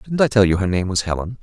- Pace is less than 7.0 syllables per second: No, 7.1 syllables/s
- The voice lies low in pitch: Yes, low, 105 Hz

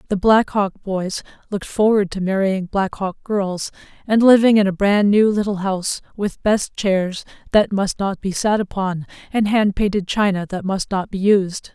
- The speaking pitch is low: No, high, 200 Hz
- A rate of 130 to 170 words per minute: No, average, 190 wpm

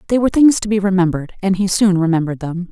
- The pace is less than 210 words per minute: No, fast, 245 wpm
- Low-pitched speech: No, high, 190 Hz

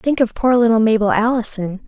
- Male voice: No, female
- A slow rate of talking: No, average, 190 wpm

